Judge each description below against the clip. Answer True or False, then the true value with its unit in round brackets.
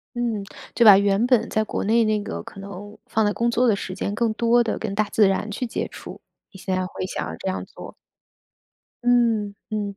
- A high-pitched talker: True (215 Hz)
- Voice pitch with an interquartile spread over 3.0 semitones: False (2.6 semitones)